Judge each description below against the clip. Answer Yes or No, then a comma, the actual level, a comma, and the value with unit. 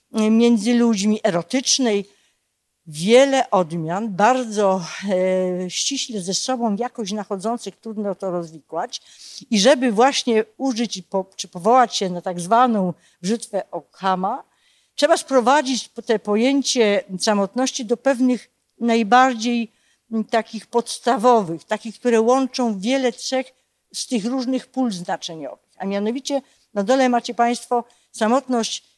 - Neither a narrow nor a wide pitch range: Yes, average, 4.0 semitones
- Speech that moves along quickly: No, average, 115 wpm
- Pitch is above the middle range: Yes, high, 230 Hz